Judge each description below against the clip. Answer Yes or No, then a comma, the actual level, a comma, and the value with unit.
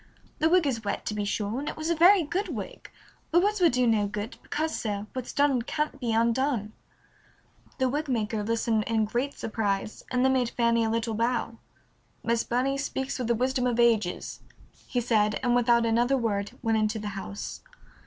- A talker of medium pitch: No, high, 235 Hz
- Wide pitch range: No, average, 3.3 semitones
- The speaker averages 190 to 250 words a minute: Yes, average, 195 wpm